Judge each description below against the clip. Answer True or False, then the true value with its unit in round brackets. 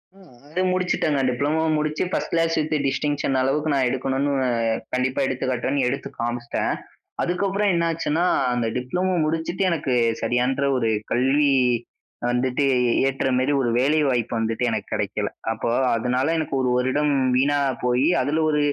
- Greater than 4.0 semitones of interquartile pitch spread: False (3.6 semitones)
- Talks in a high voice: False (135 Hz)